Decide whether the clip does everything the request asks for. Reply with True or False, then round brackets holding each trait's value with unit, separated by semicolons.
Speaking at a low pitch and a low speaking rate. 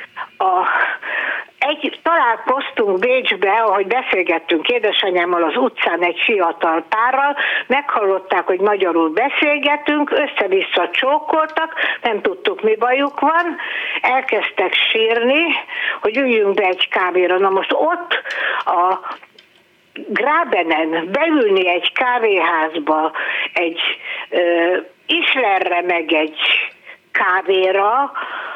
False (240 Hz; 90 wpm)